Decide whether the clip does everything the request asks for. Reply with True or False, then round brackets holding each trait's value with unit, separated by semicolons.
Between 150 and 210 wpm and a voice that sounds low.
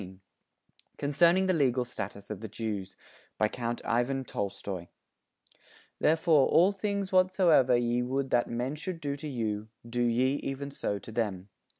True (155 wpm; 125 Hz)